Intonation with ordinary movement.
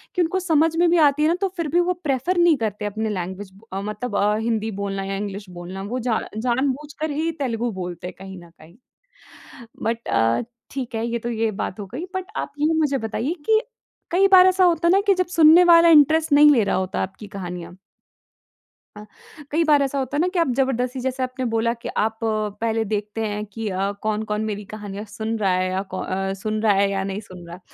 No: wide, 6.8 semitones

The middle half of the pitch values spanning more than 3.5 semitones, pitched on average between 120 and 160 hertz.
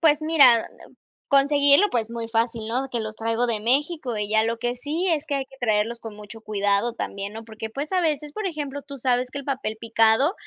No: average, 4.2 semitones; high, 245 Hz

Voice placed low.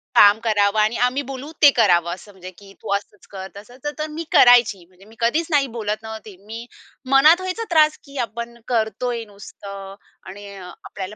No: high, 220 Hz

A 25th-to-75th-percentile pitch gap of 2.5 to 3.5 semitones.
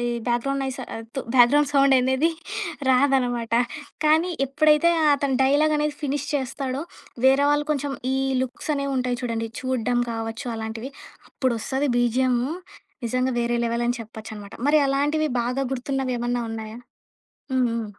Yes: average, 2.8 semitones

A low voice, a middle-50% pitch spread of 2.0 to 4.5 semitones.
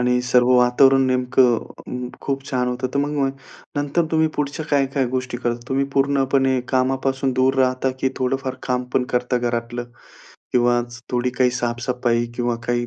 No: low, 130 Hz; narrow, 1.6 semitones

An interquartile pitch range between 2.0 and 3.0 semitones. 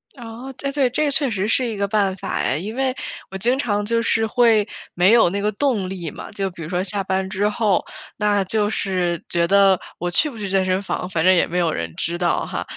No: average, 3.6 semitones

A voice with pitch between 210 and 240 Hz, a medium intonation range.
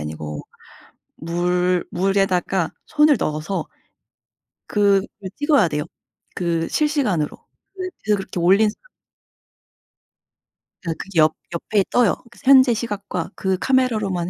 No: high, 190 Hz; average, 5.0 semitones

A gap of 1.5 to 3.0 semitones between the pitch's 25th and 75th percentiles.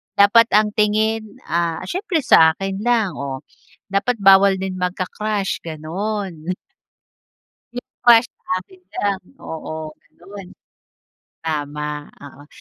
No: average, 4.8 semitones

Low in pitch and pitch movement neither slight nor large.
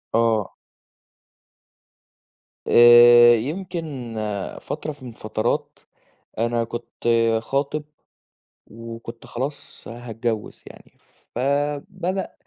Yes: low, 120 Hz; average, 3.7 semitones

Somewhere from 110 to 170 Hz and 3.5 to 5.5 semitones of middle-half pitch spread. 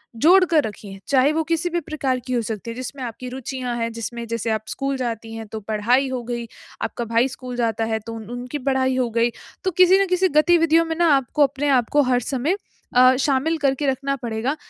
No: very high, 255 Hz; average, 3.8 semitones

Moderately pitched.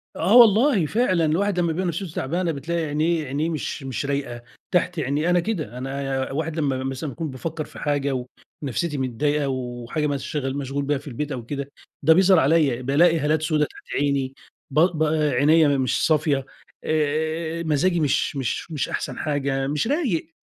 Yes: medium, 150 Hz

